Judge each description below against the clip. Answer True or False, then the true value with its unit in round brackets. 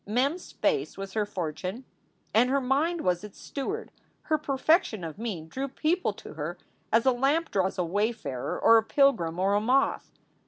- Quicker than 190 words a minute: False (185 wpm)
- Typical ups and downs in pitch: False (6.3 semitones)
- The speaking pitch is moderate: False (235 Hz)